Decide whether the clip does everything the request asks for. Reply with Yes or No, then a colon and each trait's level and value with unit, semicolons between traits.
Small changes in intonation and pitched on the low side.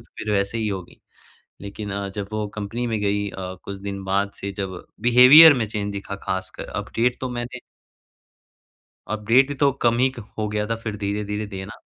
No: average, 3.0 semitones; low, 105 Hz